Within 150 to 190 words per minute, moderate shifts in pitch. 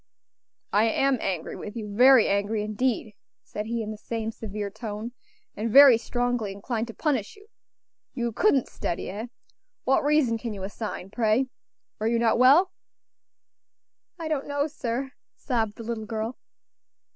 Yes: average, 155 wpm; average, 3.3 semitones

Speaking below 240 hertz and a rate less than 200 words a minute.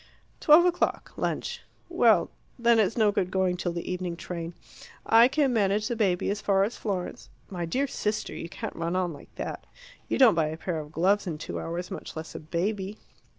No: high, 190 Hz; fast, 205 wpm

